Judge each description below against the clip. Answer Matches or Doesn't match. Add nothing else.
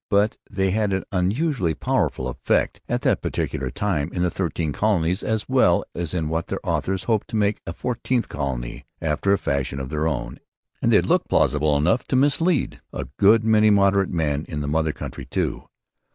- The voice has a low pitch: Matches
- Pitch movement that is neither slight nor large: Doesn't match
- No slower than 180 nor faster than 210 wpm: Matches